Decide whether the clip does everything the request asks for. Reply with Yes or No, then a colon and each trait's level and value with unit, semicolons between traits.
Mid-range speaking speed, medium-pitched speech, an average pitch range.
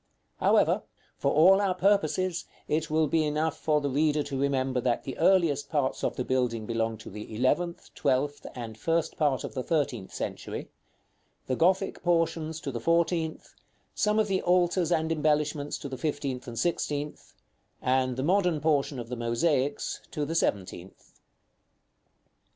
Yes: average, 160 wpm; medium, 150 Hz; average, 4.3 semitones